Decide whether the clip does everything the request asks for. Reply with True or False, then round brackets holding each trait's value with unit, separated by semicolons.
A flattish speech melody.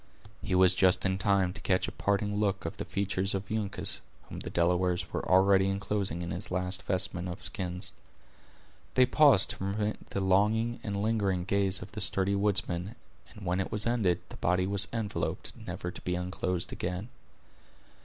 True (2.0 semitones)